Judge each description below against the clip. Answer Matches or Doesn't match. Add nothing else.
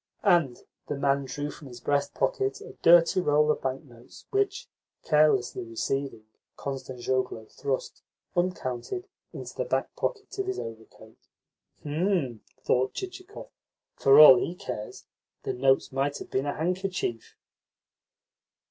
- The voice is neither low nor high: Matches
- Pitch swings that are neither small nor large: Doesn't match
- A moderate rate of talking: Doesn't match